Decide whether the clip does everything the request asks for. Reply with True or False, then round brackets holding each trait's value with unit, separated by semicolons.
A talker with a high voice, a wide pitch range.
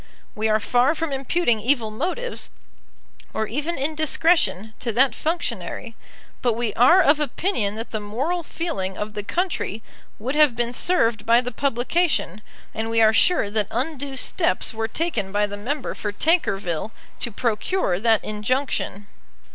True (240 Hz; 6.1 semitones)